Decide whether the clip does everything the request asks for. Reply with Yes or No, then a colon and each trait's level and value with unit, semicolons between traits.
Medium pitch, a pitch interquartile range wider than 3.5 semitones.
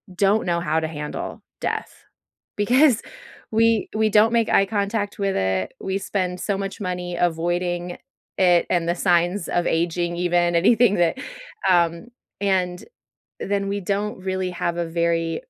No: medium, 180 Hz; average, 2.8 semitones